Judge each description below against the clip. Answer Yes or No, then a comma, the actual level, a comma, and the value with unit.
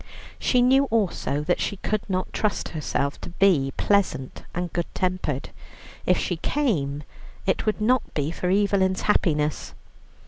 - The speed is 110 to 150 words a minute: Yes, average, 145 wpm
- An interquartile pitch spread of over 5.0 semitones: Yes, wide, 5.4 semitones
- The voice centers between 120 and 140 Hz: No, medium, 185 Hz